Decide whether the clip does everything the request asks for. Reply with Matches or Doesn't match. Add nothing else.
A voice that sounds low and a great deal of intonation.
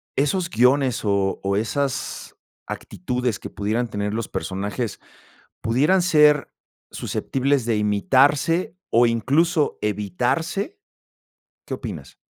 Matches